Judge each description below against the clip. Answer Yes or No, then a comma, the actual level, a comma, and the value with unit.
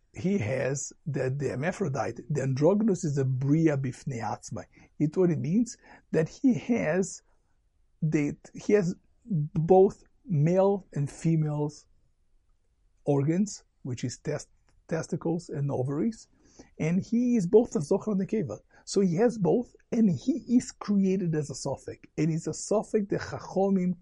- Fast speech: No, average, 145 wpm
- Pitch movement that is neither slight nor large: No, wide, 5.9 semitones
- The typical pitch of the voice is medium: Yes, medium, 165 Hz